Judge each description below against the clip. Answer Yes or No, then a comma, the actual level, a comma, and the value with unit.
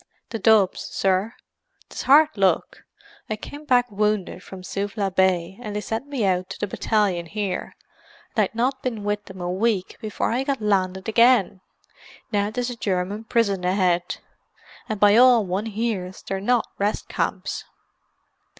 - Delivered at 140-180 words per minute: Yes, average, 160 wpm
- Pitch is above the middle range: Yes, high, 205 Hz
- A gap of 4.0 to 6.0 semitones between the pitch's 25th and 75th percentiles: No, average, 3.4 semitones